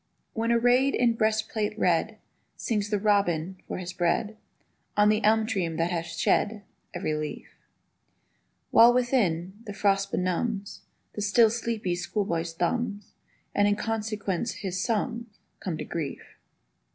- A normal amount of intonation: Yes, average, 3.9 semitones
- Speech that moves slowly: Yes, slow, 130 wpm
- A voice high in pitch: Yes, high, 205 Hz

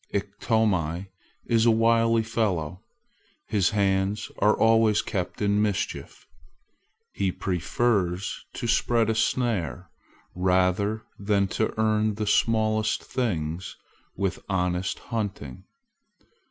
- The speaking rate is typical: No, slow, 100 wpm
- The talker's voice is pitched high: No, low, 105 Hz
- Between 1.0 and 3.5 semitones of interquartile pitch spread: Yes, average, 3.2 semitones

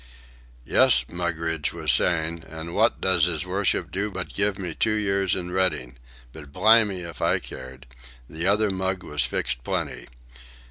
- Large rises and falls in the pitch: No, average, 3.3 semitones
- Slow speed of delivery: No, average, 155 wpm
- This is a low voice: Yes, very low, 90 Hz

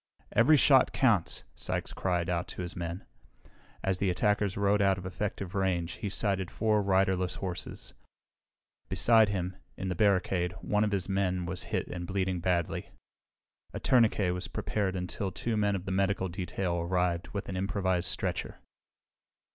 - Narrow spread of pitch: Yes, narrow, 2.0 semitones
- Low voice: Yes, very low, 95 Hz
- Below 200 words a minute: Yes, average, 165 wpm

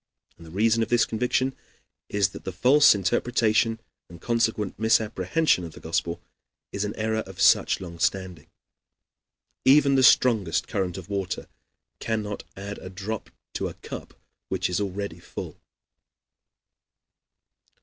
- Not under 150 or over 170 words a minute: No, average, 140 wpm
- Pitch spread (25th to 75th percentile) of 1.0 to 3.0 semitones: No, average, 3.6 semitones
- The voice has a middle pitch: No, low, 105 Hz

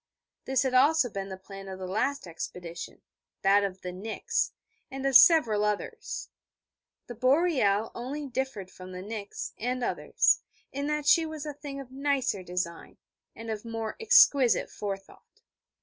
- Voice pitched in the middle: No, high, 230 Hz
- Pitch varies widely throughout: Yes, wide, 6.0 semitones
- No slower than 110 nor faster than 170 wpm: Yes, average, 155 wpm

